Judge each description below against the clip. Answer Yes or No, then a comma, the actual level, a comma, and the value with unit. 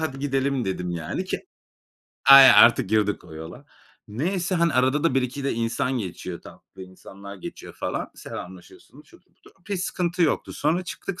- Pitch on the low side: Yes, low, 130 Hz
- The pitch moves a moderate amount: No, wide, 8.3 semitones